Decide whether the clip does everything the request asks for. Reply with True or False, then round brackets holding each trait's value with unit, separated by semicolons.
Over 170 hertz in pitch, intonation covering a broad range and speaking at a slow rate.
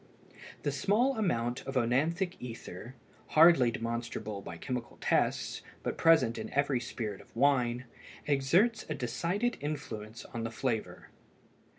False (130 Hz; 5.7 semitones; 125 wpm)